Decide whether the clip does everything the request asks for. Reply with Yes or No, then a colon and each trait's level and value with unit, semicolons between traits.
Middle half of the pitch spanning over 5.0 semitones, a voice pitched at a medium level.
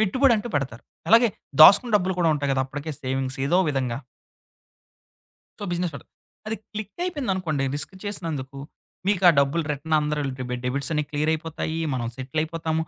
Yes: wide, 5.4 semitones; medium, 160 Hz